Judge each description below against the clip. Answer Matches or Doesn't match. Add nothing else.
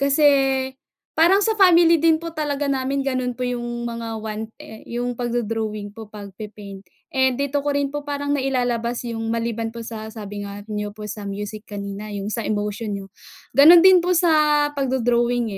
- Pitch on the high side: Matches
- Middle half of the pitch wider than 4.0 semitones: Matches